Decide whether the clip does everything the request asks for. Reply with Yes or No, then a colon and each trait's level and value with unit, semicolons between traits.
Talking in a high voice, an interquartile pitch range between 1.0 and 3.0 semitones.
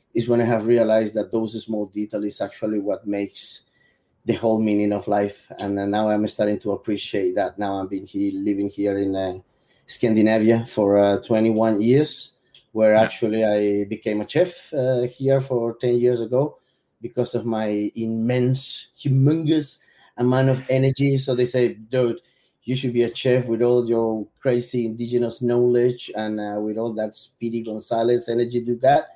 No: low, 115 Hz; average, 2.7 semitones